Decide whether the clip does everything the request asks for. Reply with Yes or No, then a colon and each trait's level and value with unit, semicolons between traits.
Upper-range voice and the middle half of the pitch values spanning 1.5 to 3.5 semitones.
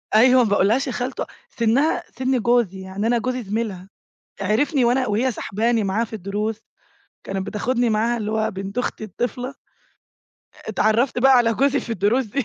Yes: high, 230 Hz; average, 3.2 semitones